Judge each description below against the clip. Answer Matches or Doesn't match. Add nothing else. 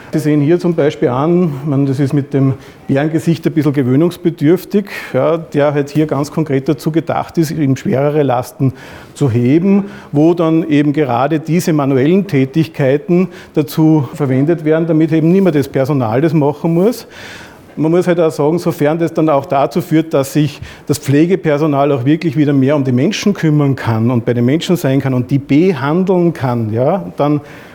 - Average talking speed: Matches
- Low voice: Doesn't match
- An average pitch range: Matches